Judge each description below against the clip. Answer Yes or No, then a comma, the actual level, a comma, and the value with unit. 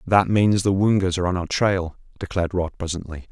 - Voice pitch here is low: Yes, very low, 90 Hz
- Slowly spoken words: No, average, 200 wpm